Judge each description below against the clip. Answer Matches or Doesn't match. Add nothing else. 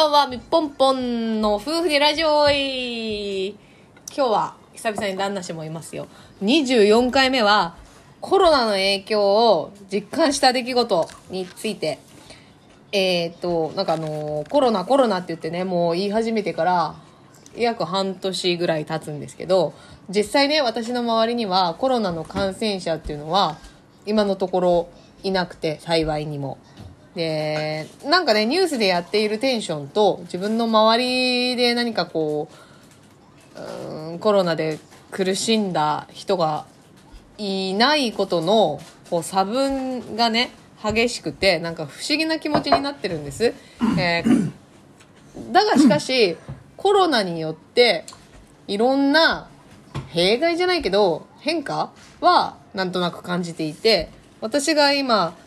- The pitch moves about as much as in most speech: Doesn't match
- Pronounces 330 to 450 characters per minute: Doesn't match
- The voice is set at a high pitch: Matches